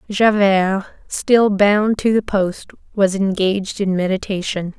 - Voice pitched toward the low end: No, high, 200 Hz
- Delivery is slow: Yes, slow, 125 wpm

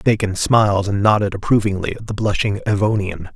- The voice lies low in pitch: Yes, low, 100 Hz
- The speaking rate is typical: Yes, average, 160 wpm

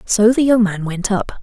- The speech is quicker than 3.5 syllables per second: Yes, 4.8 syllables/s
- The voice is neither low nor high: No, high, 210 Hz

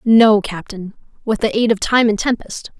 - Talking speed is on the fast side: No, average, 195 wpm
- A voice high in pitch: Yes, high, 215 Hz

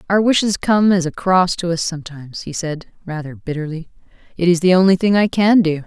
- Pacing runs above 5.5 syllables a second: Yes, 5.8 syllables/s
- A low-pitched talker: No, medium, 175 Hz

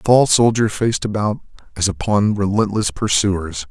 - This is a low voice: Yes, low, 100 Hz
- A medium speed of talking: Yes, average, 145 wpm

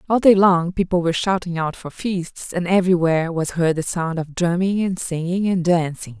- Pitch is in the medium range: Yes, medium, 175 Hz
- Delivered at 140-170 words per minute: No, fast, 205 wpm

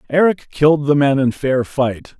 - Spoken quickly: No, average, 190 wpm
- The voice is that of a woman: No, male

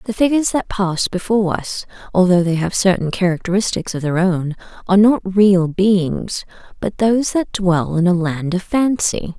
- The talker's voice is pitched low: No, high, 190 Hz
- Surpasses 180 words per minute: No, average, 175 wpm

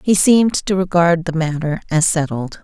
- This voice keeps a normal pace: Yes, average, 180 wpm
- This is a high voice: No, medium, 170 Hz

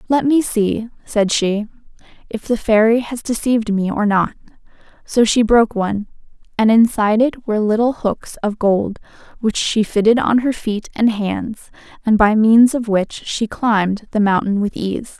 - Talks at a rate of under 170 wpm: No, average, 175 wpm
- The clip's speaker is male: No, female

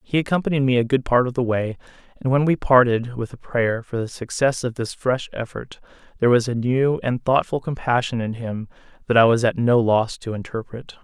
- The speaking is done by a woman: No, male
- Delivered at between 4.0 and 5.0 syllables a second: No, 5.4 syllables/s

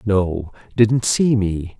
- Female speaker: No, male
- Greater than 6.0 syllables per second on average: No, 2.7 syllables/s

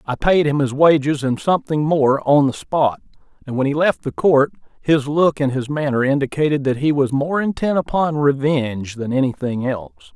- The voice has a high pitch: No, medium, 140 Hz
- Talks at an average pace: Yes, average, 195 wpm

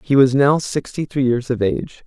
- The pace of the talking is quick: Yes, fast, 230 wpm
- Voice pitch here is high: No, low, 135 Hz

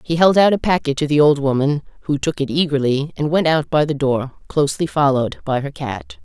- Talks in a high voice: No, medium, 150 Hz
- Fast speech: Yes, fast, 230 wpm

